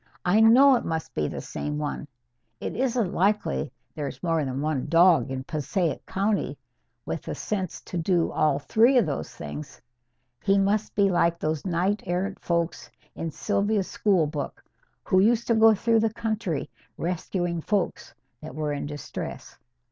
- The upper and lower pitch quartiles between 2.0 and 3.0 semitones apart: No, average, 5.3 semitones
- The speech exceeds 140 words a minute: Yes, average, 165 wpm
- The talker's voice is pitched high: No, medium, 180 Hz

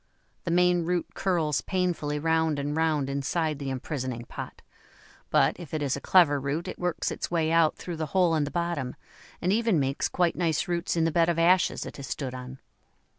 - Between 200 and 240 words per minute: Yes, fast, 205 wpm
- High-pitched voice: No, medium, 160 Hz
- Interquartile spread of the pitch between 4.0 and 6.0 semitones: No, average, 3.4 semitones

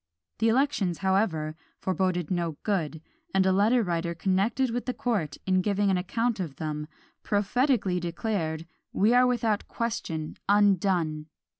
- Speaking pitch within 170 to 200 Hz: Yes, high, 190 Hz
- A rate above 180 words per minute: No, average, 140 wpm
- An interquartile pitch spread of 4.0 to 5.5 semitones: Yes, average, 4.7 semitones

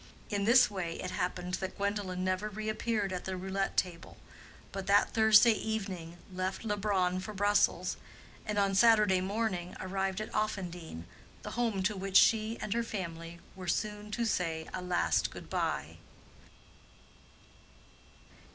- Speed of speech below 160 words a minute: Yes, average, 140 wpm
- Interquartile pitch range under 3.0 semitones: Yes, narrow, 2.6 semitones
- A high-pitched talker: Yes, high, 195 Hz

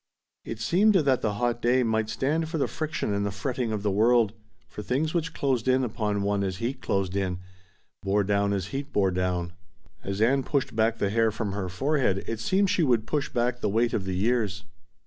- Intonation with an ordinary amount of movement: Yes, average, 4.6 semitones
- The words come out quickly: Yes, fast, 215 wpm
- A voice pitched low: Yes, low, 110 Hz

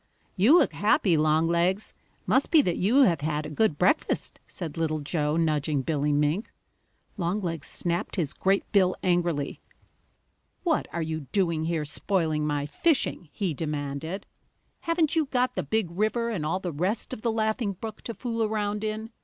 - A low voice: No, medium, 175 Hz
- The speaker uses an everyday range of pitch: No, wide, 5.8 semitones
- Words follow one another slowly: No, average, 165 wpm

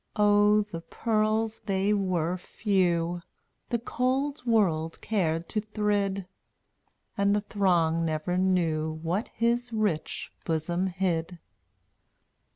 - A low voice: No, high, 195 Hz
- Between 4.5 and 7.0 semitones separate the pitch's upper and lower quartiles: No, average, 4.0 semitones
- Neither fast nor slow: No, slow, 105 wpm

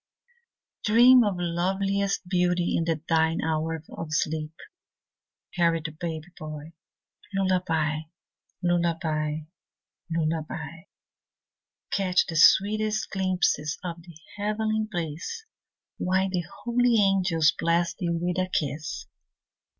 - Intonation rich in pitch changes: No, average, 3.2 semitones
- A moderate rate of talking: No, slow, 95 wpm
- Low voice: No, medium, 175 Hz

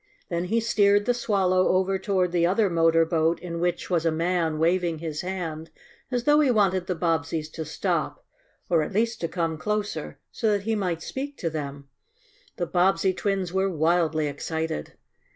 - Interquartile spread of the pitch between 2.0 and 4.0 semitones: Yes, average, 3.4 semitones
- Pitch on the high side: No, medium, 175 Hz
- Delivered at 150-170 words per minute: No, average, 180 wpm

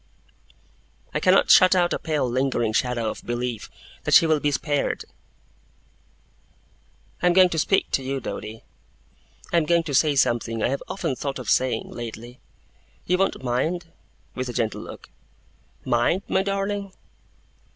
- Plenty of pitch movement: Yes, wide, 6.3 semitones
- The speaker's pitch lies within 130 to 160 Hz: Yes, medium, 140 Hz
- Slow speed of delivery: No, average, 155 wpm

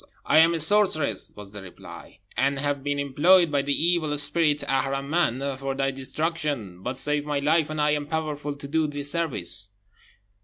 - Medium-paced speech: Yes, average, 180 wpm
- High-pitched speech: No, medium, 145 Hz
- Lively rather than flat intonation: No, narrow, 2.5 semitones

